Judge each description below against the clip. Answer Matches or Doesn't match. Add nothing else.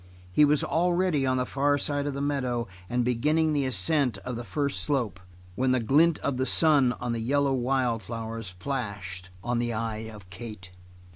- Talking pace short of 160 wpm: Doesn't match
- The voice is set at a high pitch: Doesn't match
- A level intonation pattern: Doesn't match